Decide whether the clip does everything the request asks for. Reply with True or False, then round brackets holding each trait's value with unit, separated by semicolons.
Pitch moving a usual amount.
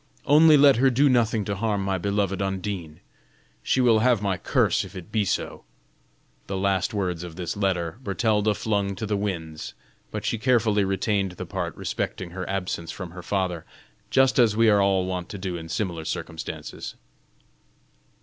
True (3.1 semitones)